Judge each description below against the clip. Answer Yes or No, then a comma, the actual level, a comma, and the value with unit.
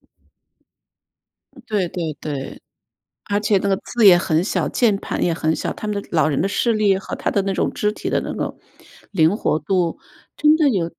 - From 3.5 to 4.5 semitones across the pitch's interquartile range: Yes, average, 4.0 semitones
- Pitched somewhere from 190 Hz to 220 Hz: Yes, high, 195 Hz